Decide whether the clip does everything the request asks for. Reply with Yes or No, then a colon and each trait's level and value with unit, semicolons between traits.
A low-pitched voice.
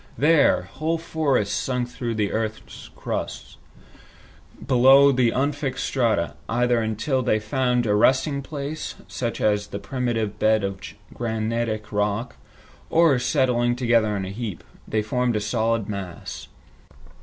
Yes: low, 120 Hz